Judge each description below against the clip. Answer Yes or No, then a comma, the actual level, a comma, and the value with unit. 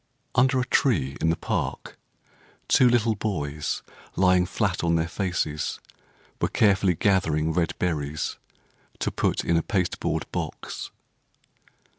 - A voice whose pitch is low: Yes, very low, 90 Hz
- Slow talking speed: Yes, slow, 125 wpm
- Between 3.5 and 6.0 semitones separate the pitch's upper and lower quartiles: Yes, average, 4.3 semitones